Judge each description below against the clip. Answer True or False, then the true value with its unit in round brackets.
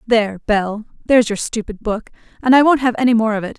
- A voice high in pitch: True (225 Hz)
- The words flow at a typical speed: False (235 wpm)